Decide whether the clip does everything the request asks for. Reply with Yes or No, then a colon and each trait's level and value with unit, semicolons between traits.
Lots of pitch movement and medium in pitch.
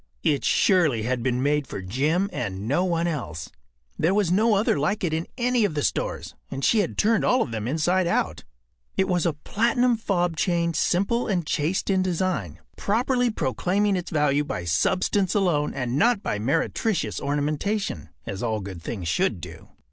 Yes: wide, 6.9 semitones; medium, 170 Hz